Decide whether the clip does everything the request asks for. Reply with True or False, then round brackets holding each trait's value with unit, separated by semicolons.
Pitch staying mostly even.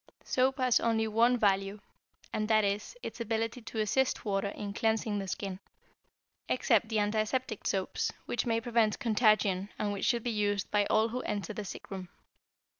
True (2.2 semitones)